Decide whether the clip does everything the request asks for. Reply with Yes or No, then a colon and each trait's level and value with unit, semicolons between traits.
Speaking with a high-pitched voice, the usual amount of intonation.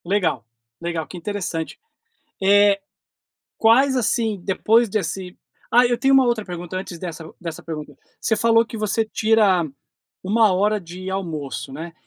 Yes: high, 195 Hz; average, 4.5 semitones